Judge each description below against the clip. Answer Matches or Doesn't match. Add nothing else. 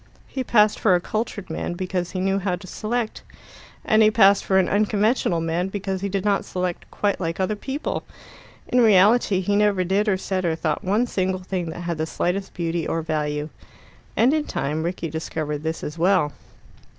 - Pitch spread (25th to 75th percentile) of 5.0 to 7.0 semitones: Doesn't match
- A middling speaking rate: Matches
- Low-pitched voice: Doesn't match